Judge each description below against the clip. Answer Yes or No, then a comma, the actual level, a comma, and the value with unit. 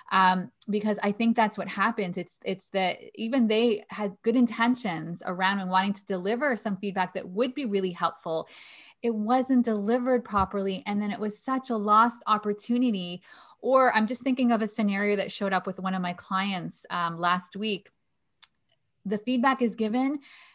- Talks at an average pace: Yes, average, 180 wpm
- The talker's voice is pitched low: No, high, 210 Hz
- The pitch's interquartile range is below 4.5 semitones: Yes, average, 3.7 semitones